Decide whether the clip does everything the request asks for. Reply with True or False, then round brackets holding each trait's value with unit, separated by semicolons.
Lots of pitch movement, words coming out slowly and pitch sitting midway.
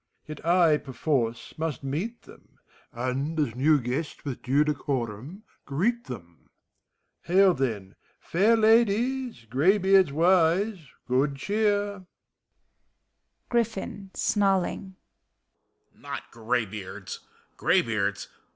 True (7.7 semitones; 95 wpm; 155 Hz)